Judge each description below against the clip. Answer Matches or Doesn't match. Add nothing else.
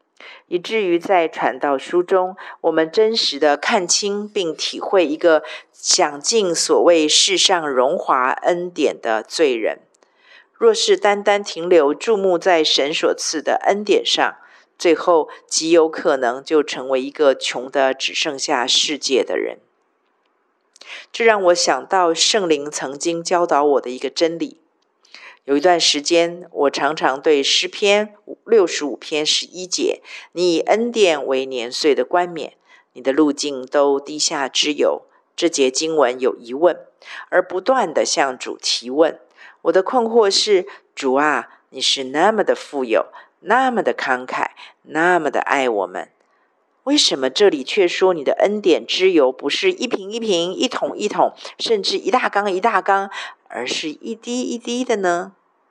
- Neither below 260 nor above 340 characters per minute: Doesn't match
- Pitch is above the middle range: Matches